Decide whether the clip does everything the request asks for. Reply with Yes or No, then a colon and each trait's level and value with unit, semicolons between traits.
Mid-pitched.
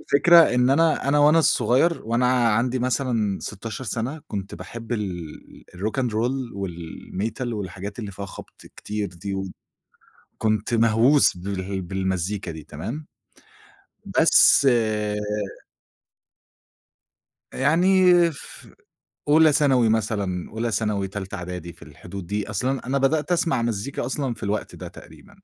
No: low, 110 Hz